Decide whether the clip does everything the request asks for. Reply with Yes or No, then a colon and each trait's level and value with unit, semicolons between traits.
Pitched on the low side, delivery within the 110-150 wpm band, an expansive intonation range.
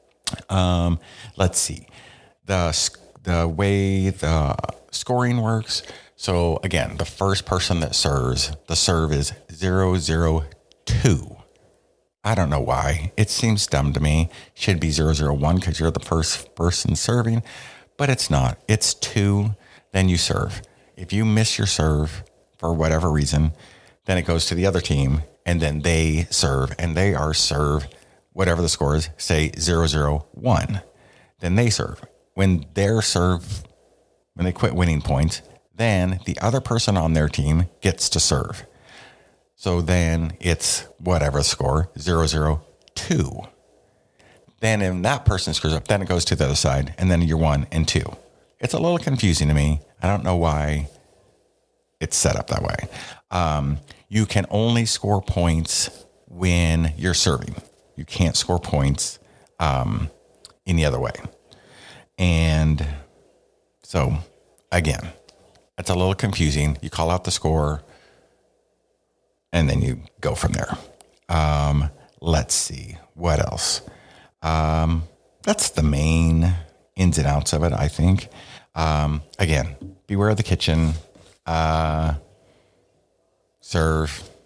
No: very low, 85 Hz; average, 145 wpm; average, 3.8 semitones